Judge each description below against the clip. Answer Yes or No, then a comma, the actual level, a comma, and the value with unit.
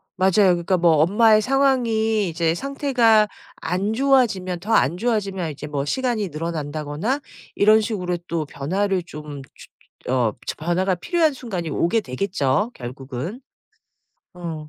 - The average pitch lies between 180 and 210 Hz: Yes, medium, 185 Hz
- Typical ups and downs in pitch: No, wide, 5.9 semitones